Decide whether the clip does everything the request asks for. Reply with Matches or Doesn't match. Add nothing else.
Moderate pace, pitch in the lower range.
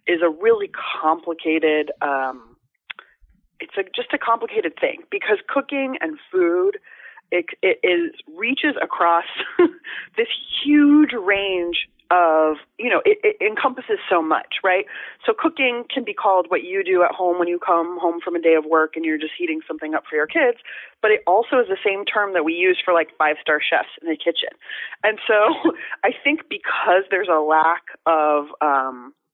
Doesn't match